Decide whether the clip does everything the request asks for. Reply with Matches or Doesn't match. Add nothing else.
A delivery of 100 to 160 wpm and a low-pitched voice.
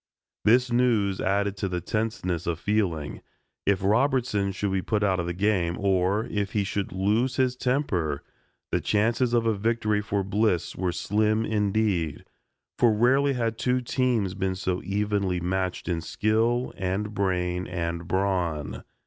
Matches